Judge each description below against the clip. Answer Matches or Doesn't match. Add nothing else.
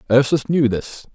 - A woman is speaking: Doesn't match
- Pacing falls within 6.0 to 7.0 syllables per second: Doesn't match